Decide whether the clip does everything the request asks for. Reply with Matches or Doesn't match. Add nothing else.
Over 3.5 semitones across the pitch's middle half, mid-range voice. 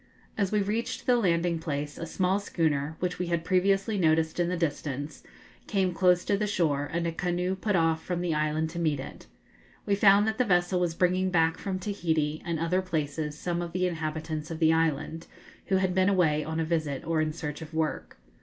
Doesn't match